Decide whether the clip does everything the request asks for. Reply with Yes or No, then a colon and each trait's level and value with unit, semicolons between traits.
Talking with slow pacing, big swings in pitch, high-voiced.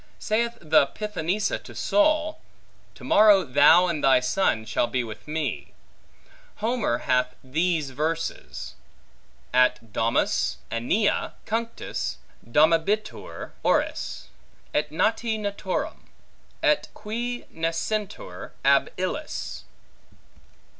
No: slow, 95 wpm; wide, 8.5 semitones; medium, 170 Hz